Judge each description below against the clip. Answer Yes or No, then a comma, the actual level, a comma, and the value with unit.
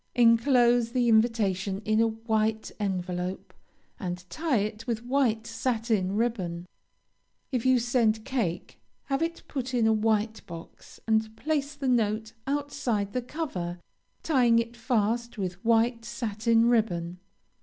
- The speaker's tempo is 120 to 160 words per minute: Yes, slow, 135 wpm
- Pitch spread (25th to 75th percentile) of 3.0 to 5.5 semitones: No, narrow, 2.6 semitones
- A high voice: Yes, high, 225 Hz